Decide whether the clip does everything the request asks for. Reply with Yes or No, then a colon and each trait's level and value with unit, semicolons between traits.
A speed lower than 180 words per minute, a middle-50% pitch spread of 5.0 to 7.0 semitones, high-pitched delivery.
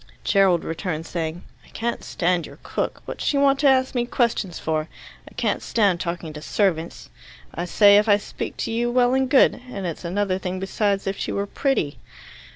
No: average, 195 wpm; wide, 5.6 semitones; high, 195 Hz